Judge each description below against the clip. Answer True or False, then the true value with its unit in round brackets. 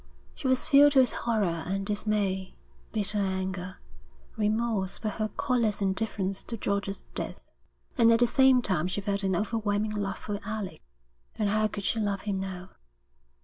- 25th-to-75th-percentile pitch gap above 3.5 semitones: False (2.5 semitones)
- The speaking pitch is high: True (205 Hz)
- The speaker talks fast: False (160 wpm)